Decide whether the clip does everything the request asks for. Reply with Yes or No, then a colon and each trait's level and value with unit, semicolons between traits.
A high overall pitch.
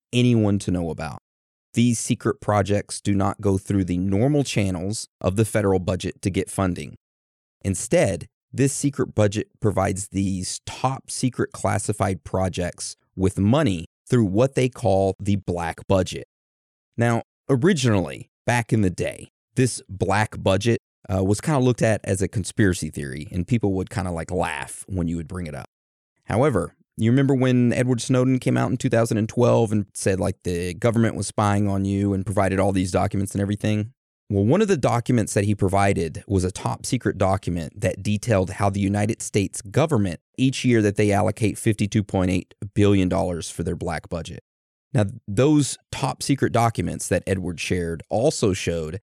No: low, 100 Hz